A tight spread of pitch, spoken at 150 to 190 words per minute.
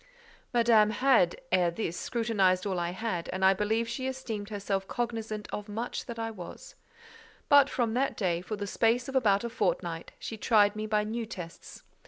No: average, 3.3 semitones; average, 185 wpm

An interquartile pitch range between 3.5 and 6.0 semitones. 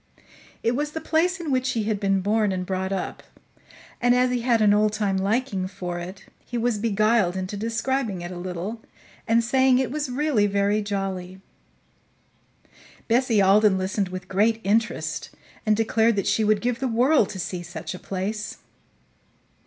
Yes: average, 3.9 semitones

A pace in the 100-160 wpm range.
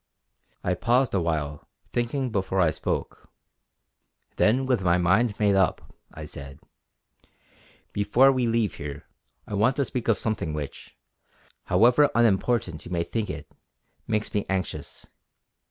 Yes: average, 140 wpm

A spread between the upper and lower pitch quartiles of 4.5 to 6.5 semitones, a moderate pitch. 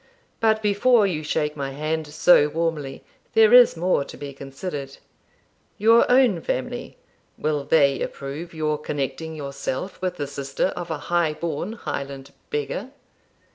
Yes: average, 4.9 semitones; medium, 155 Hz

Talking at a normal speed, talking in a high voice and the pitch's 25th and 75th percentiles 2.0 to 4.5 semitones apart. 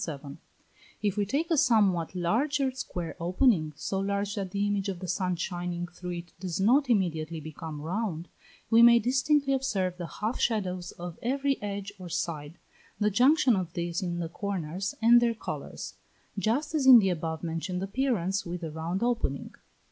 No: average, 170 wpm; high, 195 Hz; average, 5.2 semitones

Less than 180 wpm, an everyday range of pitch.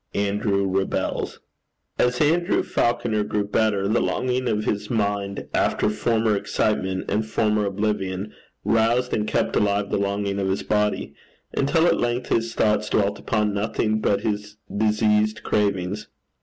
No: average, 140 wpm; narrow, 1.7 semitones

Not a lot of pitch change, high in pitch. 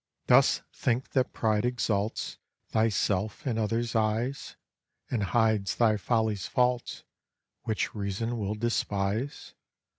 No: narrow, 2.3 semitones; low, 110 Hz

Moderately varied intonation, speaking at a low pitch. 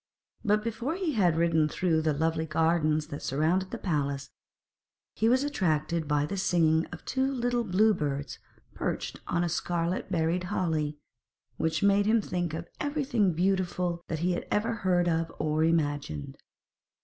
No: average, 4.2 semitones; medium, 170 Hz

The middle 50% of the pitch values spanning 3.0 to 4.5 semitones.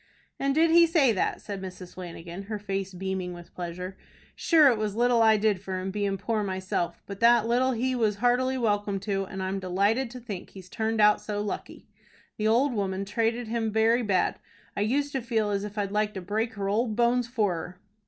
Yes: average, 3.5 semitones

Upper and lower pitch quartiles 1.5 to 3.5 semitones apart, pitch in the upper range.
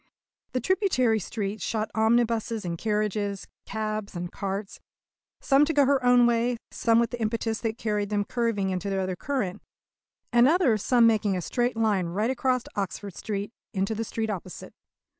Yes: average, 3.0 semitones; high, 220 Hz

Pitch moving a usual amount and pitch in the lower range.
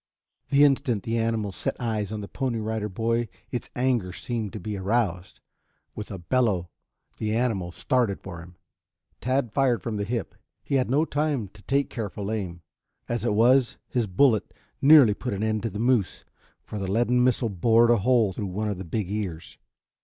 Yes: average, 3.5 semitones; low, 110 Hz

